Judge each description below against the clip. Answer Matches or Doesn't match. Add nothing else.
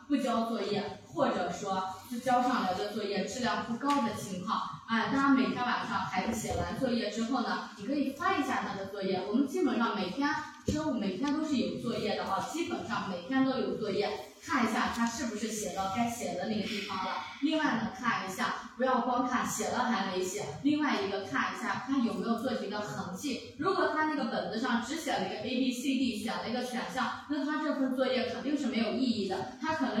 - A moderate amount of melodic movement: Matches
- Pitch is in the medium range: Doesn't match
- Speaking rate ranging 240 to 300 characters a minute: Doesn't match